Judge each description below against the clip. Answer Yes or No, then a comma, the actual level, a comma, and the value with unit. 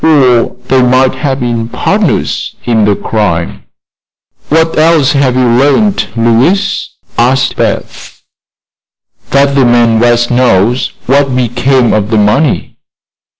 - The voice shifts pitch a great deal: No, average, 3.0 semitones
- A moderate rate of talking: No, slow, 120 wpm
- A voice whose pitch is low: Yes, low, 125 Hz